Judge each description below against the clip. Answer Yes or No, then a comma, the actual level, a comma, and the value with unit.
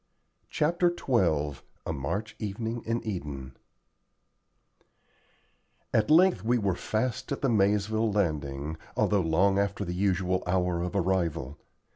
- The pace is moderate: No, slow, 120 wpm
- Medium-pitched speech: No, low, 100 Hz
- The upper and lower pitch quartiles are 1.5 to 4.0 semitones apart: No, average, 4.7 semitones